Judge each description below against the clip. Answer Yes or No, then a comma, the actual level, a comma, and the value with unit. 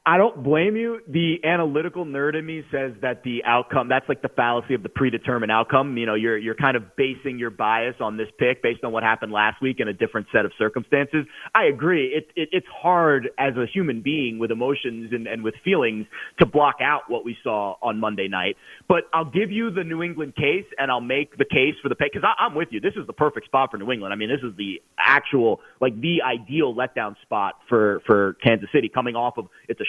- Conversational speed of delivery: No, fast, 235 wpm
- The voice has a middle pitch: No, low, 130 Hz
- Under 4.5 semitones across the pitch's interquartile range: No, average, 4.8 semitones